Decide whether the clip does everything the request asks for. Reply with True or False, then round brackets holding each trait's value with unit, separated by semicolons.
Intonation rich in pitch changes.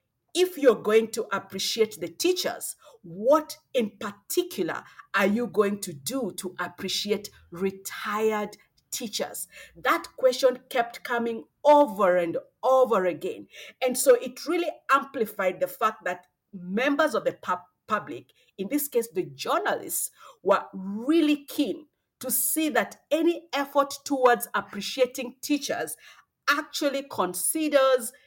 True (6.4 semitones)